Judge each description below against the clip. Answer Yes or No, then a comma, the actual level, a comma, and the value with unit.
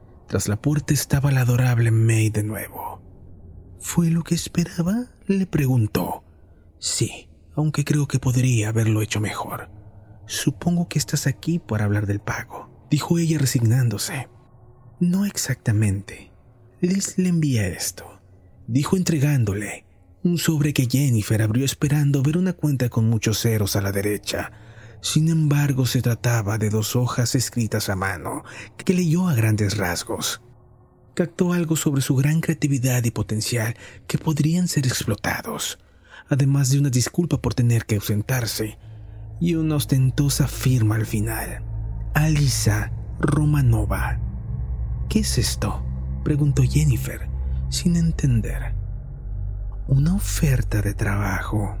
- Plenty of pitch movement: Yes, wide, 5.7 semitones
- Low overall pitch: Yes, low, 120 Hz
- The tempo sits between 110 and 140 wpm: Yes, average, 130 wpm